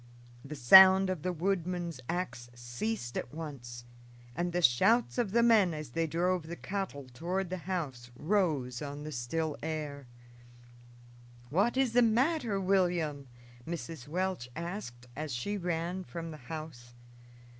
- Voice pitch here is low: No, medium, 165 Hz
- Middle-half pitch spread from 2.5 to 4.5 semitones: No, average, 4.9 semitones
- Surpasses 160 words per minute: No, average, 145 wpm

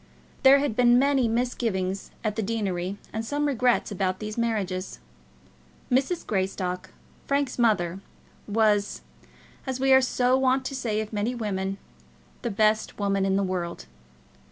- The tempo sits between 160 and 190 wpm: No, average, 145 wpm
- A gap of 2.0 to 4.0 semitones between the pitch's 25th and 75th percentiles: No, average, 4.5 semitones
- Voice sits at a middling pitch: No, high, 220 Hz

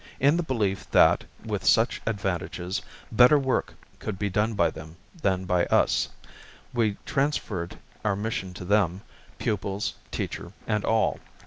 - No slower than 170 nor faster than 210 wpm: No, average, 140 wpm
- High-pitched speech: No, low, 100 Hz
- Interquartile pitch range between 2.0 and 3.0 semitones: No, average, 3.4 semitones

